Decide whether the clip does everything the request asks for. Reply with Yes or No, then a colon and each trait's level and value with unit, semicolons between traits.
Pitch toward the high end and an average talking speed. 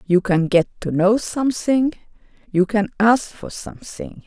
Yes: high, 210 Hz; average, 155 wpm